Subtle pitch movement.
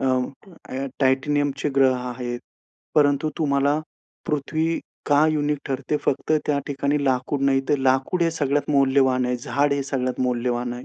Yes: narrow, 2.1 semitones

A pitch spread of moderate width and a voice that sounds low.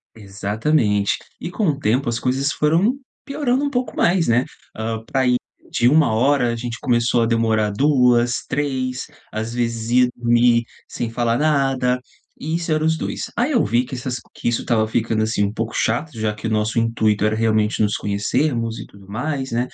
Yes: average, 3.9 semitones; low, 120 Hz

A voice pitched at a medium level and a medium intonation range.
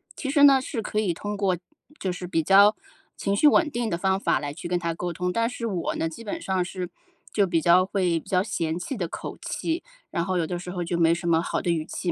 Yes: medium, 180 Hz; average, 3.3 semitones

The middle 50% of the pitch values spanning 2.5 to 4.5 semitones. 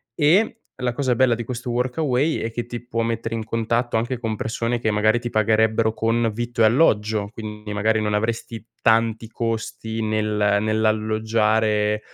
No: narrow, 1.6 semitones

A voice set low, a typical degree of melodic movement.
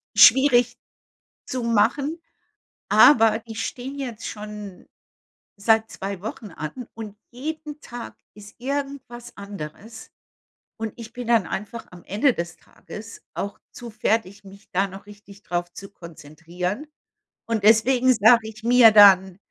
No: high, 220 Hz; average, 3.4 semitones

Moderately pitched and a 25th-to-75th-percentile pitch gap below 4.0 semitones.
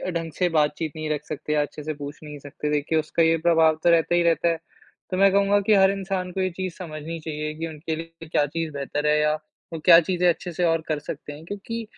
Yes: medium, 165 Hz; average, 2.8 semitones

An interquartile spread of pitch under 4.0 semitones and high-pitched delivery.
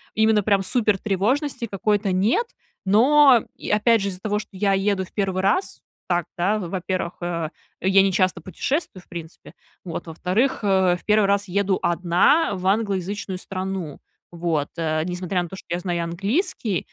Yes: average, 2.8 semitones; high, 195 Hz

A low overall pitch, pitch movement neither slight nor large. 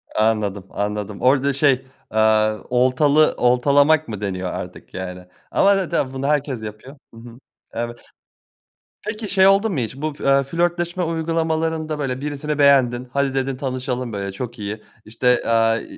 Yes: low, 130 Hz; average, 5.0 semitones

